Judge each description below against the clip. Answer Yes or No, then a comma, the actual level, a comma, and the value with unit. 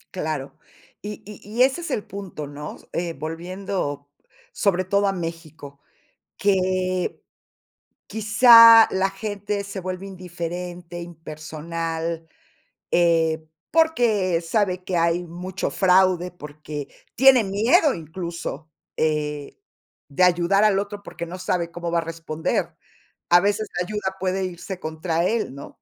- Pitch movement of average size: Yes, average, 3.3 semitones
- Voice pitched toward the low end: No, medium, 180 Hz